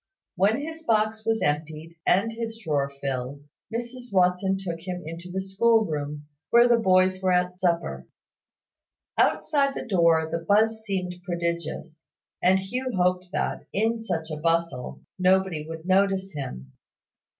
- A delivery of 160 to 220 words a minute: No, average, 145 wpm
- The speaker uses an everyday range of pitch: Yes, average, 4.8 semitones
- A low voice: No, medium, 185 Hz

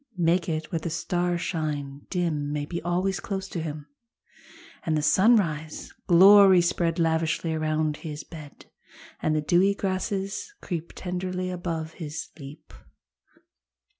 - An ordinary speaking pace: No, slow, 130 wpm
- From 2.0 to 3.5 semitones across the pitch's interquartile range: Yes, average, 2.9 semitones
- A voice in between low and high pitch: Yes, medium, 165 Hz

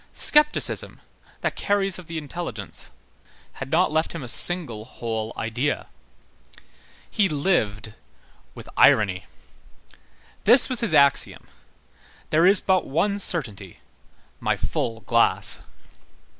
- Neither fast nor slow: No, slow, 110 wpm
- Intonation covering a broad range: Yes, wide, 8.7 semitones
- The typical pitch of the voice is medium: Yes, medium, 150 Hz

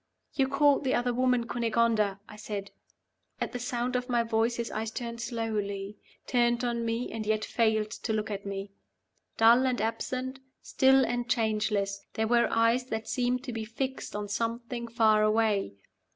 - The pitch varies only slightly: Yes, narrow, 2.2 semitones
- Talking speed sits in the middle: Yes, average, 170 wpm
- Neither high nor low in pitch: No, high, 230 Hz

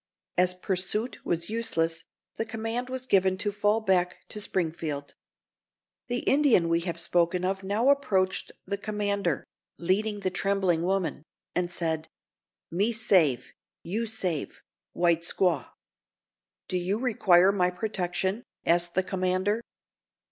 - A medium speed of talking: No, slow, 120 wpm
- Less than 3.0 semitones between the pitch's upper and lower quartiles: No, average, 3.3 semitones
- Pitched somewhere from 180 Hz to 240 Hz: Yes, medium, 185 Hz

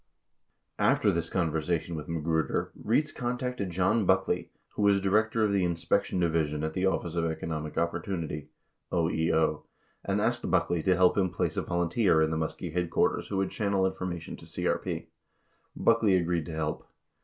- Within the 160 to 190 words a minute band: Yes, average, 170 wpm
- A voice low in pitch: Yes, very low, 85 Hz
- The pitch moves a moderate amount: Yes, average, 3.2 semitones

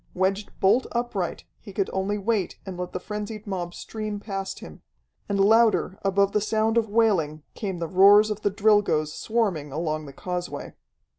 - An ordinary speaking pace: Yes, average, 170 wpm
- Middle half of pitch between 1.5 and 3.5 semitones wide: Yes, average, 2.9 semitones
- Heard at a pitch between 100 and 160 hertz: No, high, 200 Hz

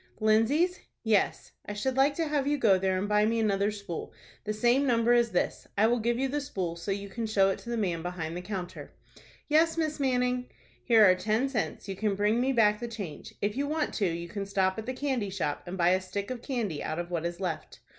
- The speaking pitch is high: Yes, high, 215 Hz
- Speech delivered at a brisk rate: Yes, fast, 245 wpm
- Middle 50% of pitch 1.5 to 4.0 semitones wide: No, average, 4.8 semitones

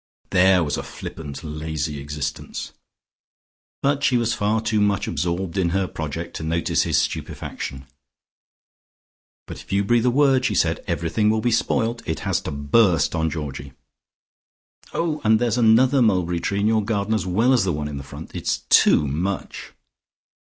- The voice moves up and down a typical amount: No, wide, 6.1 semitones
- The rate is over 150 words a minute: Yes, average, 165 wpm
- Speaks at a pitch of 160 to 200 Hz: No, very low, 95 Hz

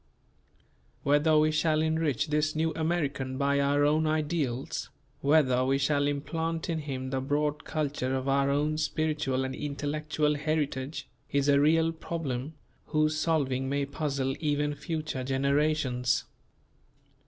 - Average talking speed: No, slow, 130 wpm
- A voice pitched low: No, medium, 145 Hz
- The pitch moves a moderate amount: No, narrow, 2.2 semitones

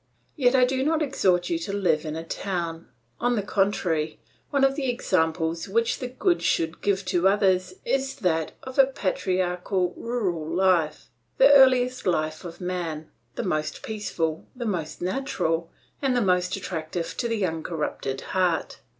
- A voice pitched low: No, medium, 185 Hz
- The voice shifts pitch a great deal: Yes, wide, 6.7 semitones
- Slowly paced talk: No, average, 160 wpm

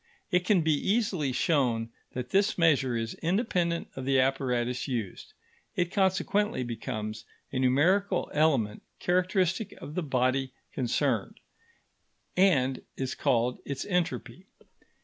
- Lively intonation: Yes, wide, 6.3 semitones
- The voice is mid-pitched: Yes, medium, 145 Hz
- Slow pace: Yes, slow, 120 wpm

